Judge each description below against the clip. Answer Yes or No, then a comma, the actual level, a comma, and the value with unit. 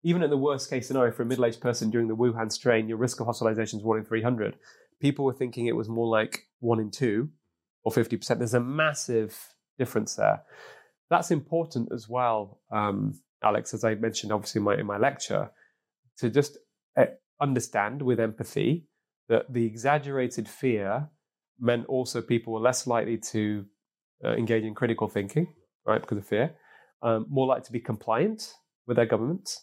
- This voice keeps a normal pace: Yes, average, 180 wpm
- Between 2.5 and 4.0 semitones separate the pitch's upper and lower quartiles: Yes, average, 2.9 semitones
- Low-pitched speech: Yes, low, 120 Hz